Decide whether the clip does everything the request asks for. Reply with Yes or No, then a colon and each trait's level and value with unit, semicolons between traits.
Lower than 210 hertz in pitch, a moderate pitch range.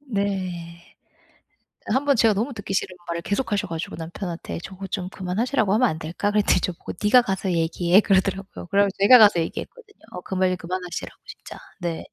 Yes: high, 190 Hz; average, 3.2 semitones